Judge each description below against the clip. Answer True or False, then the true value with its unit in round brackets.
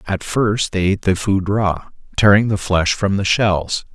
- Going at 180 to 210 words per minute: True (200 wpm)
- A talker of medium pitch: False (100 Hz)